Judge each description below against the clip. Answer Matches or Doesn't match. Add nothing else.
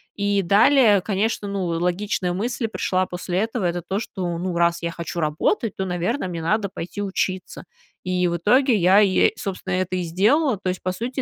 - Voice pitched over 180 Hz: Matches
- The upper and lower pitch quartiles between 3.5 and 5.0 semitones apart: Doesn't match